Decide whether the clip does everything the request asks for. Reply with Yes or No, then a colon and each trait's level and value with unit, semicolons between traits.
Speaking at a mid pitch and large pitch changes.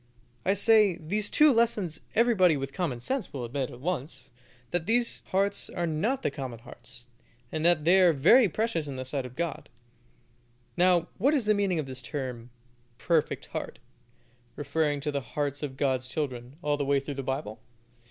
Yes: medium, 155 Hz; wide, 6.1 semitones